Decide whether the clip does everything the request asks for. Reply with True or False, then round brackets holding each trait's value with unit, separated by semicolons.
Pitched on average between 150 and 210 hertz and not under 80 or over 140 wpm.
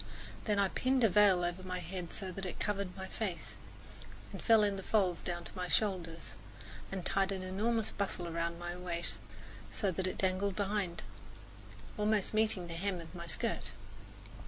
False (185 Hz; 180 wpm)